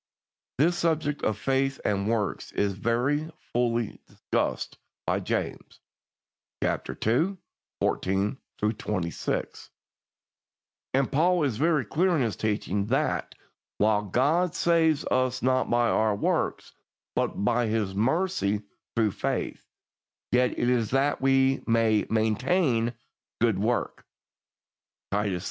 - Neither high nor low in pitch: No, low, 120 Hz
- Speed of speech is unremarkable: No, slow, 120 wpm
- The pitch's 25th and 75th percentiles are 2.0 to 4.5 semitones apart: No, average, 4.9 semitones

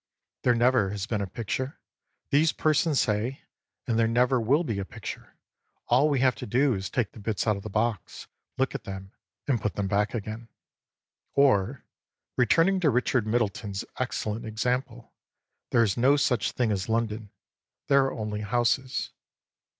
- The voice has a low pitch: Yes, low, 115 Hz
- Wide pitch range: No, average, 3.6 semitones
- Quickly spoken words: No, average, 170 wpm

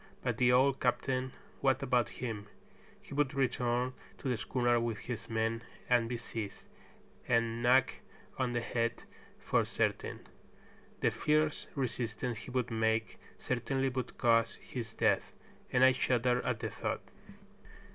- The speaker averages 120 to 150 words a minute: Yes, average, 145 wpm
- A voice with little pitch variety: Yes, narrow, 2.0 semitones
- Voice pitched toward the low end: Yes, low, 120 Hz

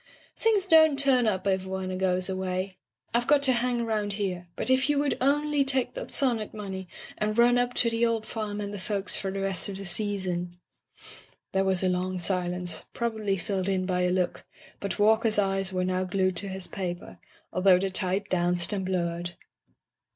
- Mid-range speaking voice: No, high, 195 Hz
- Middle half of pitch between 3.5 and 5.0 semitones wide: Yes, average, 3.8 semitones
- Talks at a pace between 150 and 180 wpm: No, average, 195 wpm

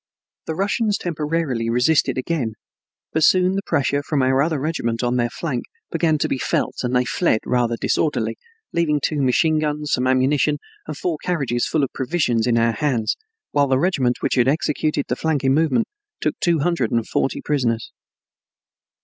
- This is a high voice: No, medium, 145 Hz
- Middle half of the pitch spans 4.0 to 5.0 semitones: Yes, average, 4.3 semitones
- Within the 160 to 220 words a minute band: Yes, average, 175 wpm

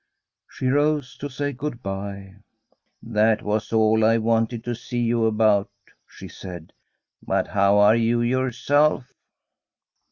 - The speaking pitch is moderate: No, low, 115 Hz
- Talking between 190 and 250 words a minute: No, average, 140 wpm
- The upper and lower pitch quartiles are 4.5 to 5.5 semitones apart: No, average, 3.0 semitones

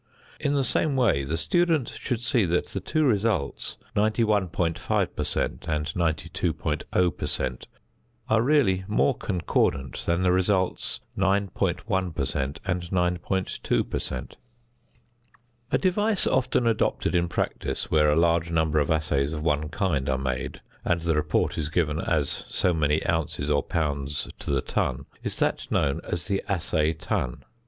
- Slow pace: No, average, 155 wpm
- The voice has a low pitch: Yes, very low, 85 Hz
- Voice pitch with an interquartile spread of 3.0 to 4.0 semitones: No, average, 4.8 semitones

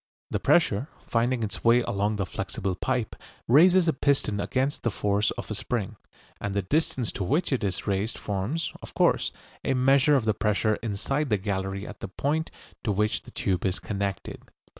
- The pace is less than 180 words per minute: No, average, 185 wpm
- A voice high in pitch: No, low, 110 Hz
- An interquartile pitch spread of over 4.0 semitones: Yes, average, 5.0 semitones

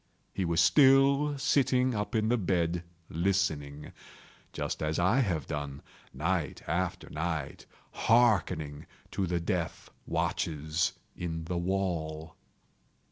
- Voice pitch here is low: Yes, very low, 85 Hz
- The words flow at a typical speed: No, slow, 110 wpm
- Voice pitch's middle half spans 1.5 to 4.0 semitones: No, wide, 5.5 semitones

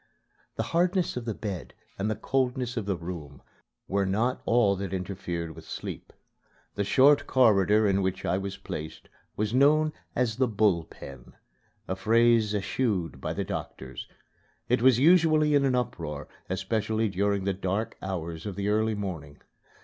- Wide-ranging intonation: No, average, 4.7 semitones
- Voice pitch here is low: Yes, low, 105 Hz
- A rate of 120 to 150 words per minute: No, average, 160 wpm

